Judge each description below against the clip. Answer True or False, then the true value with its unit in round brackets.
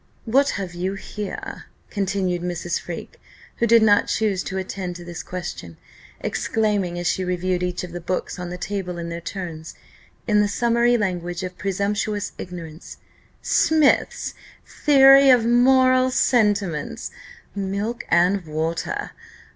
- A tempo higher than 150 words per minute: False (140 wpm)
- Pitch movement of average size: True (3.8 semitones)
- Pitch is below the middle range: False (190 Hz)